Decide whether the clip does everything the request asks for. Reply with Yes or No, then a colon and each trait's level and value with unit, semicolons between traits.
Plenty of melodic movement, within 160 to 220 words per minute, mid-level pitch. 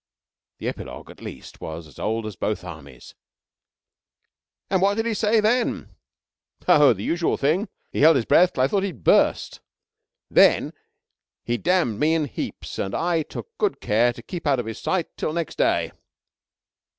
Yes: wide, 8.8 semitones; average, 175 wpm; medium, 155 Hz